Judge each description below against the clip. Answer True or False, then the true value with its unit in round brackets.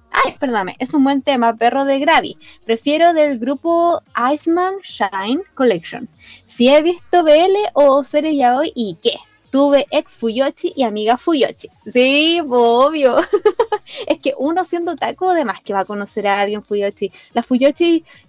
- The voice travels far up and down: True (5.9 semitones)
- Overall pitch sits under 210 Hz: False (280 Hz)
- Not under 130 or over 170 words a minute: True (160 wpm)